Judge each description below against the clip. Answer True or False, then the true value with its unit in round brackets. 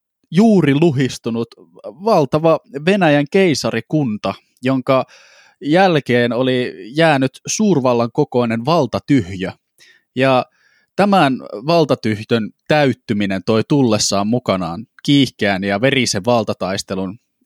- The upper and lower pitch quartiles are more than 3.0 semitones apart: True (5.4 semitones)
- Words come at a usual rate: False (80 wpm)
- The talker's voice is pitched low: True (130 Hz)